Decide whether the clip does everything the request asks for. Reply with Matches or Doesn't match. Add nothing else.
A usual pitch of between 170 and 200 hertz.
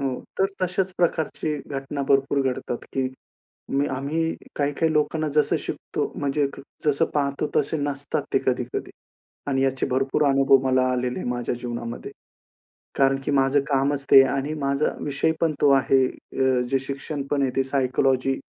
Doesn't match